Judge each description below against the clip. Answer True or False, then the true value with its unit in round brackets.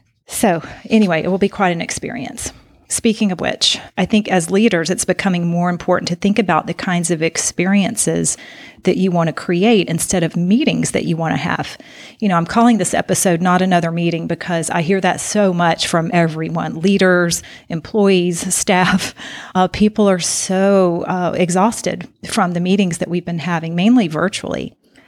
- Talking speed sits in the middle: True (175 wpm)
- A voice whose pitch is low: False (180 Hz)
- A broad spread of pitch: False (2.5 semitones)